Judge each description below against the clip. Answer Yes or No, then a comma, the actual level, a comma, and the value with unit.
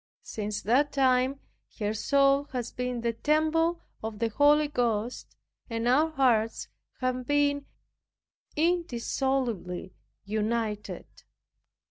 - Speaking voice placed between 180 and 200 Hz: No, very high, 250 Hz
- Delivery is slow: Yes, slow, 100 wpm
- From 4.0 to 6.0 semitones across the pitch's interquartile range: Yes, average, 4.3 semitones